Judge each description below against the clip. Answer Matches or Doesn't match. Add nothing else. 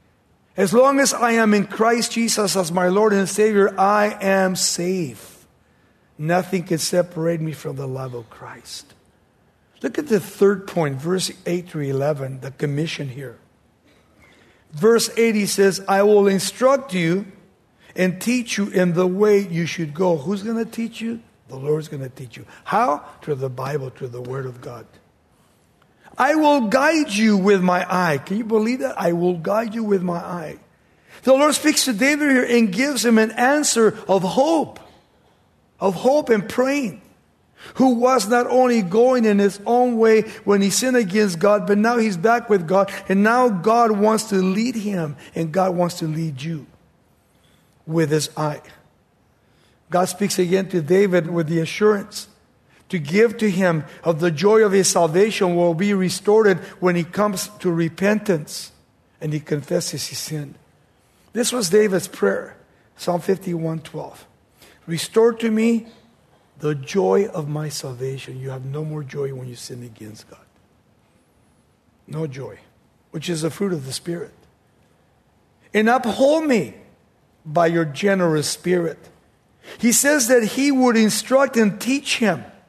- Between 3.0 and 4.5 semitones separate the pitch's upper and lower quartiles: Doesn't match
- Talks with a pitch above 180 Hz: Matches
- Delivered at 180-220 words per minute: Doesn't match